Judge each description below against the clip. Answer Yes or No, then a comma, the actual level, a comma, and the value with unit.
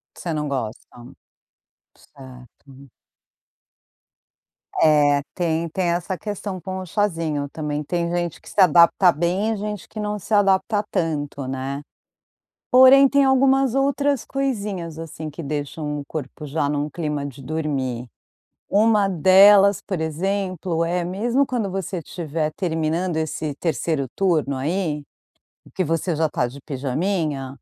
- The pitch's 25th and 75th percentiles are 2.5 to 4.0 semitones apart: No, average, 4.9 semitones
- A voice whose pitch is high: No, medium, 165 Hz